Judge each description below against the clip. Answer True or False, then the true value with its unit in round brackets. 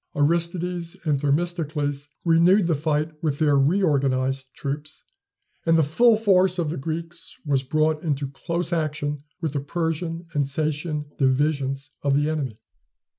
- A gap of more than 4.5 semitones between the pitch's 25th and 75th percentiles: False (2.9 semitones)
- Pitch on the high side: False (155 Hz)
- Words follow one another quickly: False (140 wpm)